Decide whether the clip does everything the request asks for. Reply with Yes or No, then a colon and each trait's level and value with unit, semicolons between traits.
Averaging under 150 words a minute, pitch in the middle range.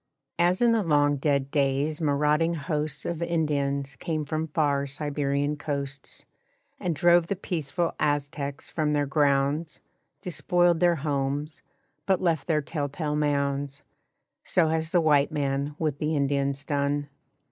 Yes: average, 140 wpm; medium, 150 Hz